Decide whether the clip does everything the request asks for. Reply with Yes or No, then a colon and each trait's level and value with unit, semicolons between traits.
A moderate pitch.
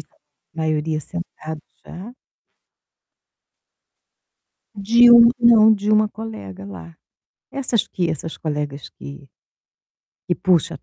Yes: medium, 175 Hz